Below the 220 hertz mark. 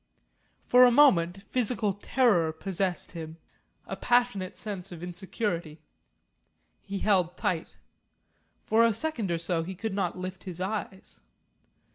Yes: high, 190 Hz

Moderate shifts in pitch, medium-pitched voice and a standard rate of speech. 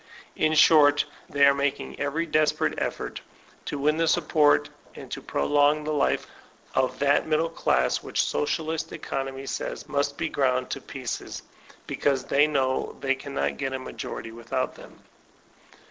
No: narrow, 2.1 semitones; medium, 145 Hz; average, 150 wpm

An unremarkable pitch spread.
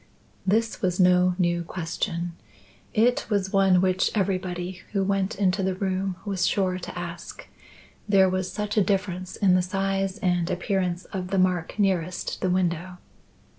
No: narrow, 1.4 semitones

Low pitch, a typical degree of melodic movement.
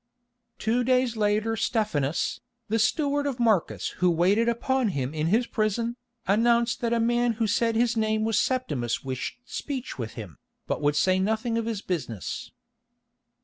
No: high, 220 Hz; average, 4.6 semitones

